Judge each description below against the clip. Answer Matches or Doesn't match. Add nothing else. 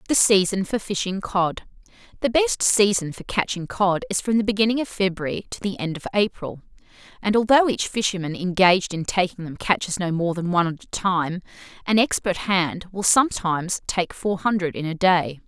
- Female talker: Matches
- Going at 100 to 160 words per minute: Doesn't match